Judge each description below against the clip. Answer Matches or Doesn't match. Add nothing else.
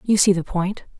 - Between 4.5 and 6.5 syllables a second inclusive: Matches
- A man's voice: Doesn't match